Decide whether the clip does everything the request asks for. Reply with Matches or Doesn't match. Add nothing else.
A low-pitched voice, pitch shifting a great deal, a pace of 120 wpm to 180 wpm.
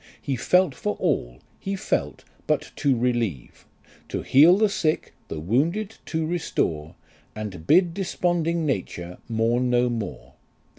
Matches